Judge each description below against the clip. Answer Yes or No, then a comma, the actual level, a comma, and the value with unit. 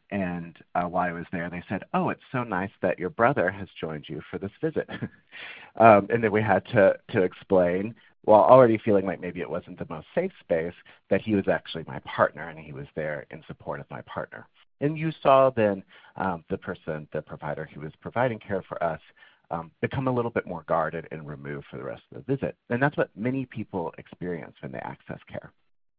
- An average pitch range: No, wide, 5.8 semitones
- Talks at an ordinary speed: No, fast, 220 wpm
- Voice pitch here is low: Yes, low, 100 Hz